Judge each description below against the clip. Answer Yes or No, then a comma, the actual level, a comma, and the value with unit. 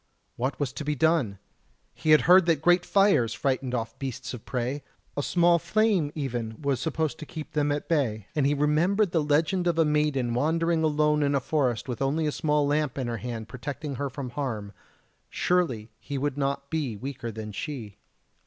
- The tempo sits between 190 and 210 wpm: Yes, average, 195 wpm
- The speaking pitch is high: No, medium, 145 Hz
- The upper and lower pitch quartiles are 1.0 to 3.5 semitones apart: No, average, 4.1 semitones